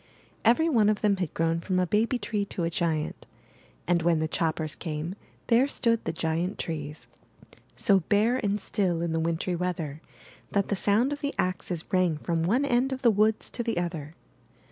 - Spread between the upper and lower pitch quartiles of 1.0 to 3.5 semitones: No, average, 4.9 semitones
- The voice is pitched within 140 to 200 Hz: Yes, medium, 185 Hz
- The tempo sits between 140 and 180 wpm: No, average, 190 wpm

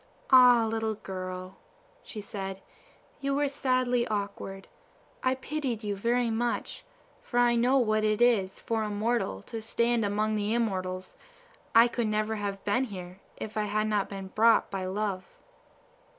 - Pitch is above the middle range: Yes, high, 215 Hz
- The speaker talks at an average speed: Yes, average, 155 wpm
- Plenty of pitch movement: No, average, 3.2 semitones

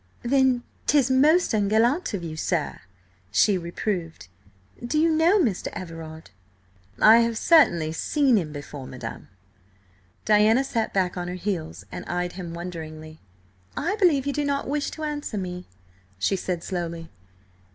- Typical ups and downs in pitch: No, wide, 8.4 semitones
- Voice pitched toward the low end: No, high, 195 Hz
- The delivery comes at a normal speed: Yes, average, 145 wpm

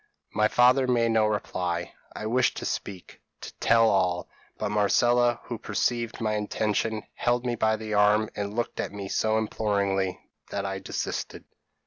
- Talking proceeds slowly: No, average, 165 wpm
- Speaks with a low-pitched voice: Yes, low, 110 Hz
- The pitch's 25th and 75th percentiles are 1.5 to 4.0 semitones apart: Yes, narrow, 2.5 semitones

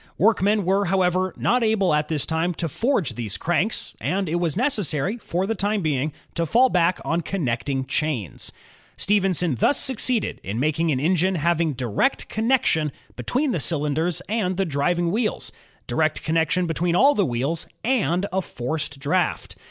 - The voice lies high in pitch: No, medium, 175 Hz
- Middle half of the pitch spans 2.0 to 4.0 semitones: No, average, 4.7 semitones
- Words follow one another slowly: No, average, 165 wpm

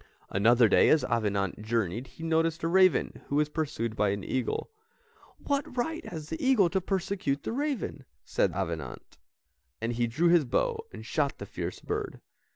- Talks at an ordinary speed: Yes, average, 170 wpm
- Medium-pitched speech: Yes, medium, 155 Hz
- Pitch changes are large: Yes, wide, 8.8 semitones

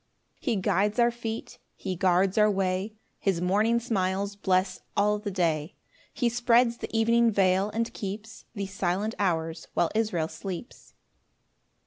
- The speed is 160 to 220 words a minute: No, average, 145 wpm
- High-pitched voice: Yes, high, 200 Hz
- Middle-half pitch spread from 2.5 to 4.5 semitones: Yes, average, 3.3 semitones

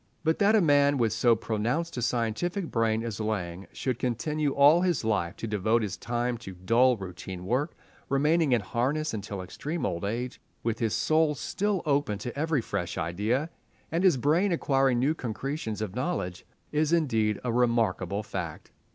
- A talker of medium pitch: No, low, 120 Hz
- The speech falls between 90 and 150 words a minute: No, average, 170 wpm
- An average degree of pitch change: No, wide, 5.8 semitones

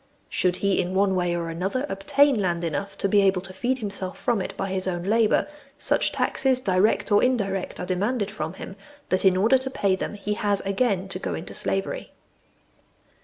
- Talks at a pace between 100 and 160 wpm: No, average, 200 wpm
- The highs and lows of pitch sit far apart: No, narrow, 2.5 semitones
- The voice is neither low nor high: No, high, 195 Hz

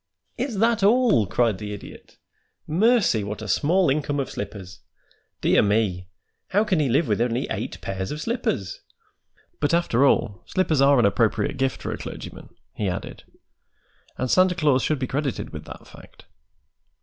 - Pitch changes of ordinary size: No, wide, 8.7 semitones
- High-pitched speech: No, low, 135 Hz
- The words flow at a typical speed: Yes, average, 165 wpm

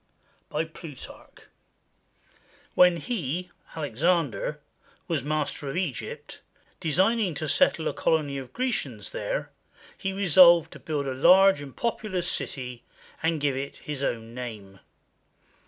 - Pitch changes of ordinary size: Yes, average, 4.8 semitones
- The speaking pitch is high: No, medium, 155 Hz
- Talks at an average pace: No, slow, 125 wpm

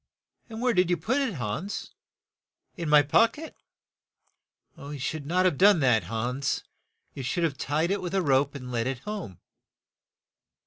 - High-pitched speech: No, medium, 155 Hz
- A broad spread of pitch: Yes, wide, 6.5 semitones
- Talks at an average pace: Yes, average, 185 wpm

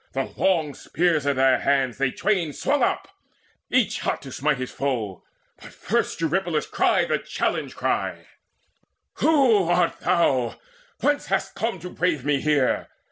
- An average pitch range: No, wide, 5.7 semitones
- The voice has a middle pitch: Yes, medium, 155 Hz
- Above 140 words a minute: Yes, average, 150 wpm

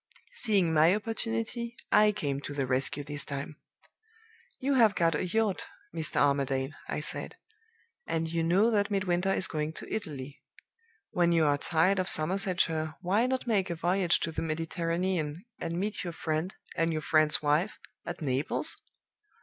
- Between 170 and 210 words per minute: No, average, 160 wpm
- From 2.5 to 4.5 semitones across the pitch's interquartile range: Yes, average, 4.2 semitones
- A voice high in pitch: No, medium, 170 Hz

